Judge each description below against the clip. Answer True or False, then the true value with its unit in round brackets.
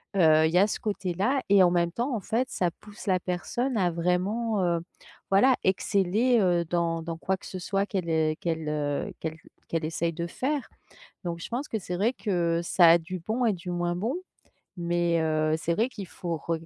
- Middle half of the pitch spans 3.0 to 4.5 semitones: True (3.6 semitones)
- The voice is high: False (180 Hz)